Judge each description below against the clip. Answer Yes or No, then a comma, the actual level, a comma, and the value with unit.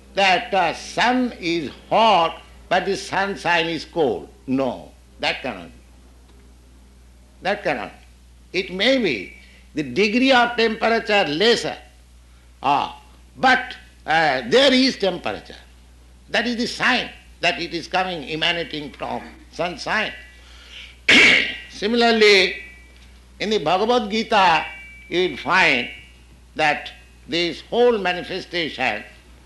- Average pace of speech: No, slow, 110 wpm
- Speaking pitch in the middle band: Yes, medium, 165 Hz